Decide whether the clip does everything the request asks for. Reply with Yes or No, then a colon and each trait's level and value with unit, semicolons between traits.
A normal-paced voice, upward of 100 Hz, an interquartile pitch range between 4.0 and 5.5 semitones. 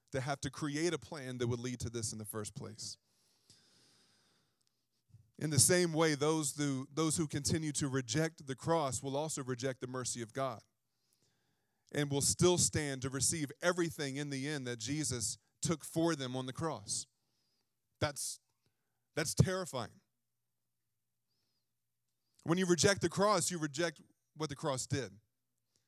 Yes: average, 155 wpm; medium, 140 Hz; average, 4.5 semitones